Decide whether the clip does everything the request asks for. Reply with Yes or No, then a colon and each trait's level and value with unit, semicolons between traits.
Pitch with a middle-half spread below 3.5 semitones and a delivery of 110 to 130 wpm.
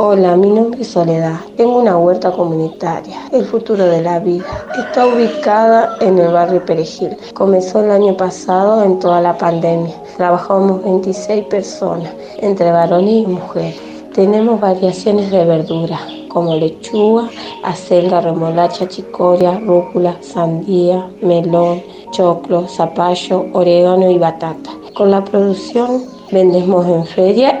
Yes: average, 2.9 semitones; slow, 125 wpm